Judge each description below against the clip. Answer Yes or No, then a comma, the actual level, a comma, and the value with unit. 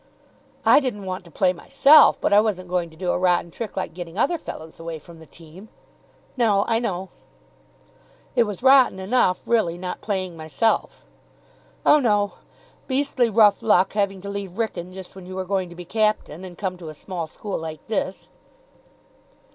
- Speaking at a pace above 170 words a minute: Yes, average, 180 wpm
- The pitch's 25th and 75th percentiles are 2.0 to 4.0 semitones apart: Yes, average, 3.6 semitones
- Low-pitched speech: No, high, 190 Hz